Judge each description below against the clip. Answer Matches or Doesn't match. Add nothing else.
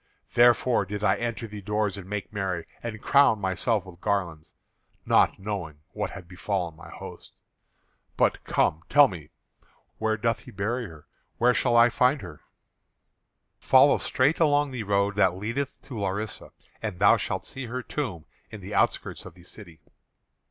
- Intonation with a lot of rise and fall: Doesn't match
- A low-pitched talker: Matches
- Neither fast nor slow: Matches